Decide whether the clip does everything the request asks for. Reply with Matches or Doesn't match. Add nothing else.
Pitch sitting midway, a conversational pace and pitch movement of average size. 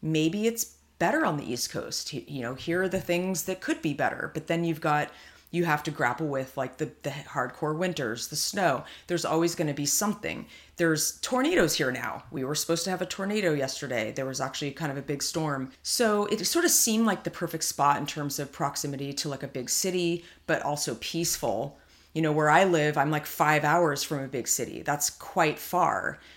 Doesn't match